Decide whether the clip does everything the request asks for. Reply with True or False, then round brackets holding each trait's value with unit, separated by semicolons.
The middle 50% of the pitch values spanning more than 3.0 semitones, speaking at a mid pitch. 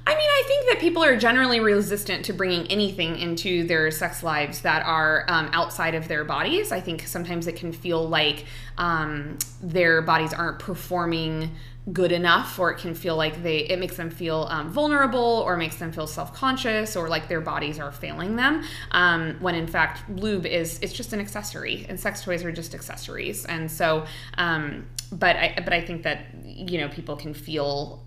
False (2.6 semitones; 170 Hz)